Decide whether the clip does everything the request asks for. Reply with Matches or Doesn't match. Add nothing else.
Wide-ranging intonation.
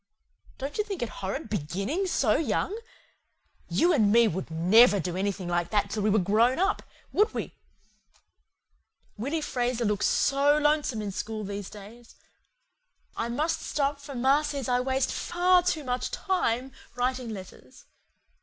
Matches